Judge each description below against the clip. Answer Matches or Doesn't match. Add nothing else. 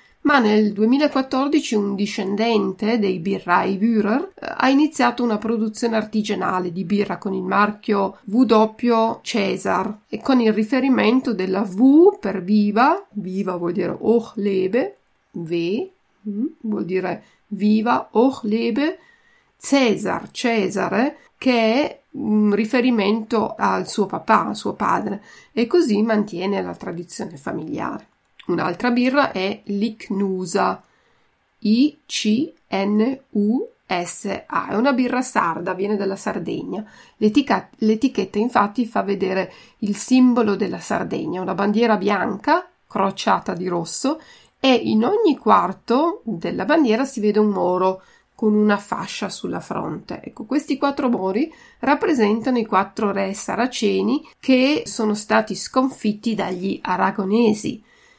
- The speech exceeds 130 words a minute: Doesn't match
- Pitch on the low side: Doesn't match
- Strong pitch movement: Doesn't match